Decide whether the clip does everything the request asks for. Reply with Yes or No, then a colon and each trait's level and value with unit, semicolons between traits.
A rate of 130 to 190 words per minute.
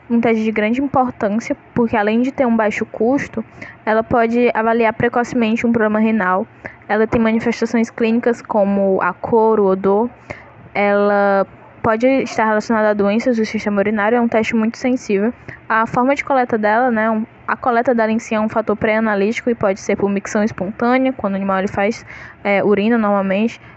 Yes: average, 180 wpm